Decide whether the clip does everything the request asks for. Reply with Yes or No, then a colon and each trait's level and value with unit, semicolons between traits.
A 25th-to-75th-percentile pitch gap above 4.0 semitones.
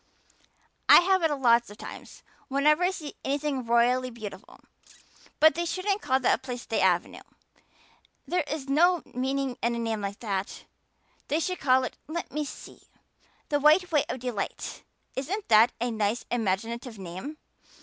Yes: average, 4.8 semitones